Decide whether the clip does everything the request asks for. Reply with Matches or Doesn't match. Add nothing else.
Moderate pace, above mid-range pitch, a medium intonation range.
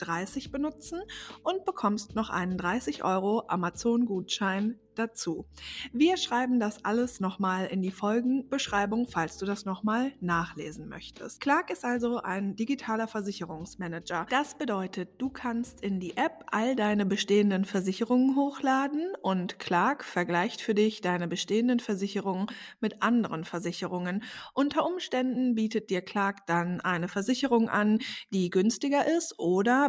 Matches